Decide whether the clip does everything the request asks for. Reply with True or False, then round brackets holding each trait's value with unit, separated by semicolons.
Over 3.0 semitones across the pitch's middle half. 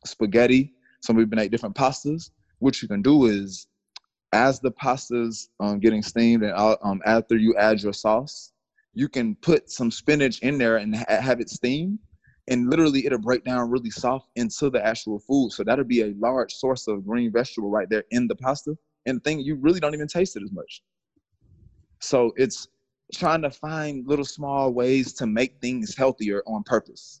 True (4.0 semitones)